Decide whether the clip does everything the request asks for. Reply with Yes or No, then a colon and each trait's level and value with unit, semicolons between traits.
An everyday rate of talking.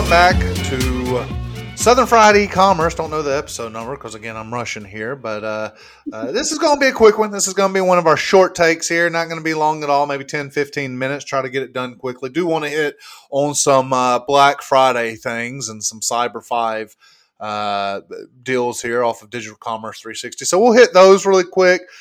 No: fast, 220 wpm